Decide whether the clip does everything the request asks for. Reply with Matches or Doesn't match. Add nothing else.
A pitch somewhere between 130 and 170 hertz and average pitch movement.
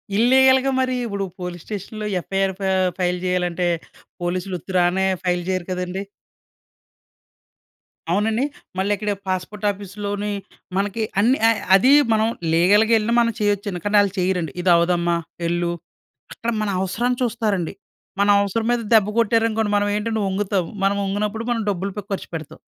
Doesn't match